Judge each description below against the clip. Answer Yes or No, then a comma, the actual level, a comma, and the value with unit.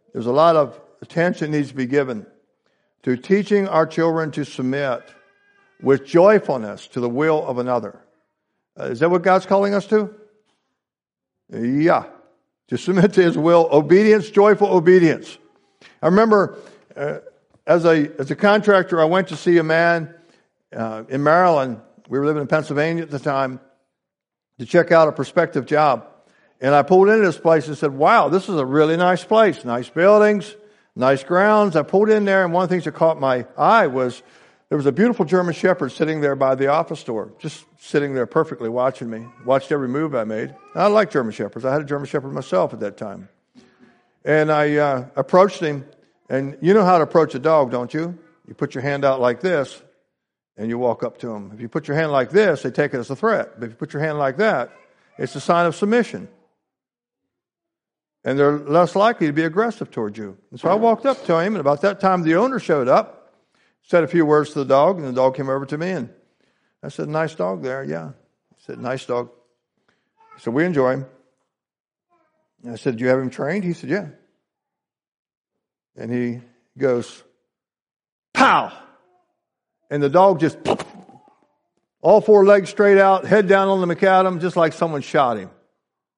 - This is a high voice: No, medium, 155 Hz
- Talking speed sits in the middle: Yes, average, 195 wpm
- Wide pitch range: Yes, wide, 5.8 semitones